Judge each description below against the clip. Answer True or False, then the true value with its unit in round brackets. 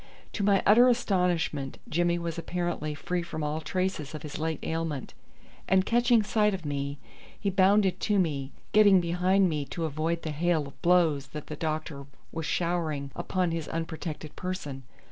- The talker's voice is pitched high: False (170 Hz)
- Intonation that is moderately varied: True (3.5 semitones)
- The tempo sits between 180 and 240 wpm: False (165 wpm)